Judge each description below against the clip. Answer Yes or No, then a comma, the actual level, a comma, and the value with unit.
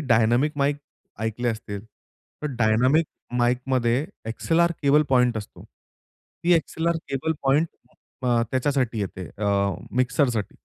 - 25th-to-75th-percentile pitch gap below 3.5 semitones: No, average, 3.8 semitones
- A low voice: Yes, low, 125 Hz